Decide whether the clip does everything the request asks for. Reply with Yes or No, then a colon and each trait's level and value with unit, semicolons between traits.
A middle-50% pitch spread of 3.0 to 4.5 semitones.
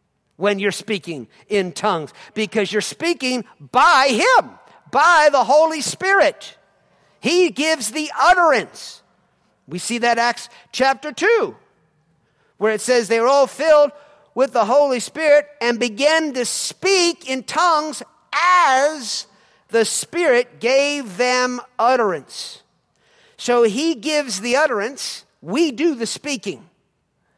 No: average, 5.3 semitones